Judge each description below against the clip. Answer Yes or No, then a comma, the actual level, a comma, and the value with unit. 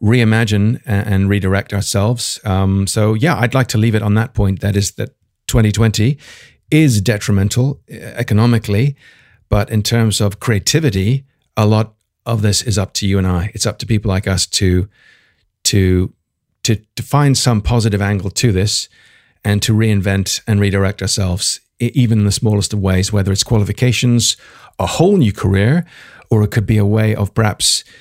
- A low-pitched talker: Yes, low, 110 Hz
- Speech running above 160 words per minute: Yes, average, 170 wpm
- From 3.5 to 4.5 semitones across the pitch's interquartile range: No, average, 2.9 semitones